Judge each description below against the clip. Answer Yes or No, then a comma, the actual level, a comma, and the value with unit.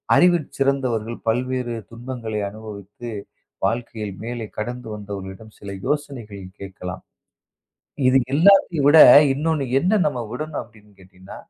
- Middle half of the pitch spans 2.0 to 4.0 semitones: No, average, 4.6 semitones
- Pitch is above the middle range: No, low, 120 Hz